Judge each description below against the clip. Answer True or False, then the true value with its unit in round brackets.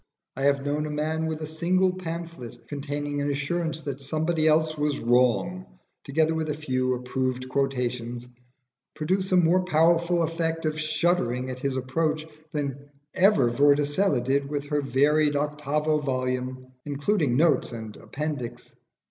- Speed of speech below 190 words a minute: True (145 wpm)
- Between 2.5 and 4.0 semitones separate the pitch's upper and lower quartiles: True (3.5 semitones)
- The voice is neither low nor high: True (145 Hz)